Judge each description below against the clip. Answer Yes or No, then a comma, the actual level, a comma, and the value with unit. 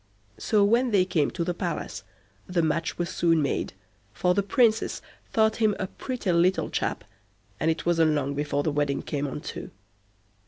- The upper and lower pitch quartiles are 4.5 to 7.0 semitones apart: Yes, average, 5.1 semitones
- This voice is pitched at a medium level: Yes, medium, 170 Hz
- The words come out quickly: No, average, 180 wpm